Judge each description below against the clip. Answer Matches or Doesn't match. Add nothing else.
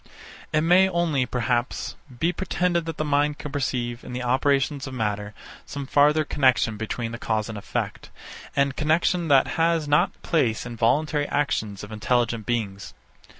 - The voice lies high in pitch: Doesn't match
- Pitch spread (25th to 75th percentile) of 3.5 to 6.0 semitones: Matches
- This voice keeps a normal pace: Matches